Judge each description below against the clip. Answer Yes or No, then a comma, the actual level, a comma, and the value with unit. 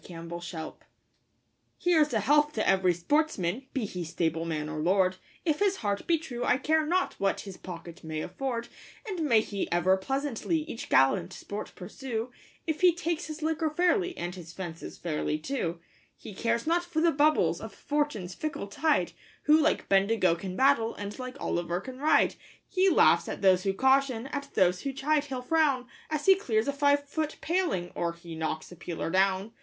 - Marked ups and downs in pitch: Yes, wide, 8.9 semitones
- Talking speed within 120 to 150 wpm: No, average, 185 wpm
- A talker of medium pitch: No, high, 235 Hz